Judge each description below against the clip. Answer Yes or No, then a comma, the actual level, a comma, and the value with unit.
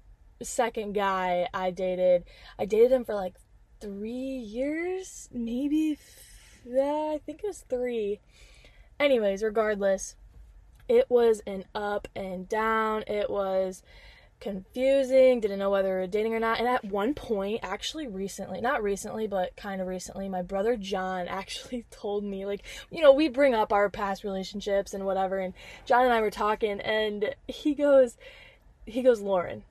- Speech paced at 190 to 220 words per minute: No, average, 160 wpm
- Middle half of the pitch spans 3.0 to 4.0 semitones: No, average, 4.5 semitones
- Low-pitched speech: No, high, 215 Hz